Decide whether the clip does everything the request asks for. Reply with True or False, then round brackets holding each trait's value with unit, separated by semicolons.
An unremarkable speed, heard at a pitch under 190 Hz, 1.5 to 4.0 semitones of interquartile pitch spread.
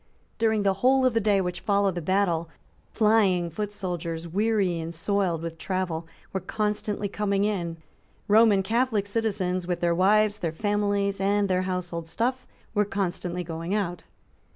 False (155 wpm; 195 Hz; 3.1 semitones)